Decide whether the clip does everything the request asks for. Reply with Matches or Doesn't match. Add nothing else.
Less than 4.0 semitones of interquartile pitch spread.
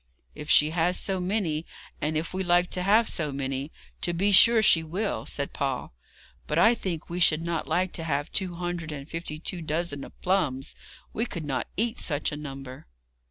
Matches